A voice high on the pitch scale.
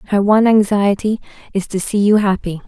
Yes: high, 200 Hz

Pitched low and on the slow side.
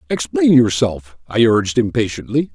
Yes: low, 110 Hz; slow, 120 wpm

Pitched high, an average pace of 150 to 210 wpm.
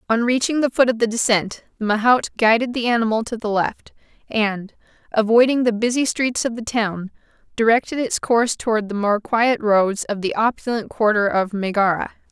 Yes: high, 225 Hz; average, 180 wpm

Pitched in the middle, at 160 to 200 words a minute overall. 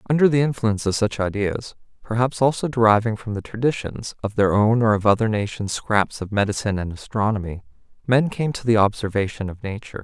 No: low, 110 Hz; average, 185 wpm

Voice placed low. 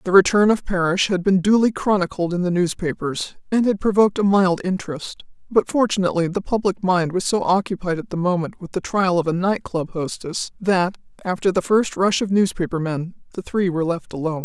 No: medium, 185 Hz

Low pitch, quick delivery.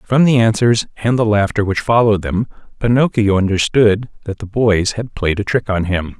No: low, 105 Hz; average, 195 wpm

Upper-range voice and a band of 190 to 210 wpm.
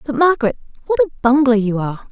Yes: high, 245 Hz; average, 200 wpm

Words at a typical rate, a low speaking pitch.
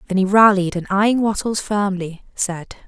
No: average, 165 wpm; high, 195 Hz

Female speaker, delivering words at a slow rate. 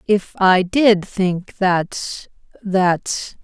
Yes: female; slow, 85 wpm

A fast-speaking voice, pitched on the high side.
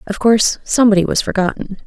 No: average, 160 wpm; high, 205 Hz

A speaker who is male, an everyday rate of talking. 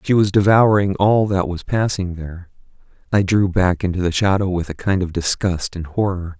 Yes: male; average, 195 wpm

